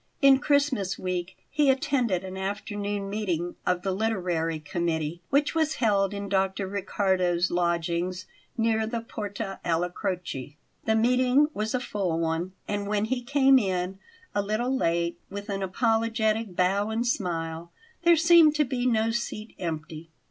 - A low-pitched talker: No, high, 200 Hz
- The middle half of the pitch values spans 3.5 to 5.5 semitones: Yes, average, 4.5 semitones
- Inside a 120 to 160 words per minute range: Yes, average, 150 wpm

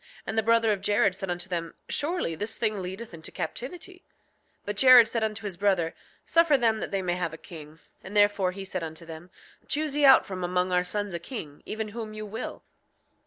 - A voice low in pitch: No, high, 205 Hz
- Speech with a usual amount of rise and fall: Yes, average, 4.0 semitones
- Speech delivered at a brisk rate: Yes, fast, 215 wpm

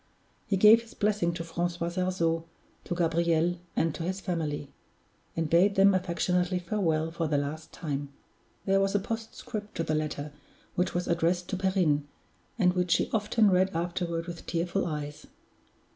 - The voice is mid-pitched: Yes, medium, 175 Hz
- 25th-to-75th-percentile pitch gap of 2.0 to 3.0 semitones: Yes, average, 2.7 semitones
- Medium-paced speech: Yes, average, 160 wpm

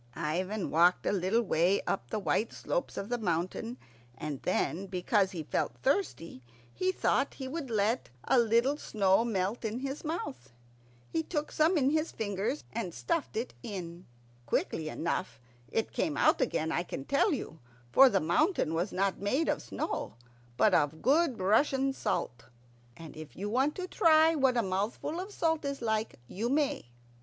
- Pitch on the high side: Yes, high, 220 Hz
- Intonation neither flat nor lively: No, wide, 7.4 semitones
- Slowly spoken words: No, average, 170 wpm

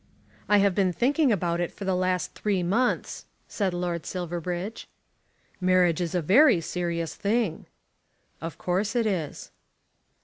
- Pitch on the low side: No, medium, 185 Hz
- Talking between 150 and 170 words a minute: No, average, 140 wpm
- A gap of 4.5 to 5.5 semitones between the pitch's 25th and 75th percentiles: No, average, 2.9 semitones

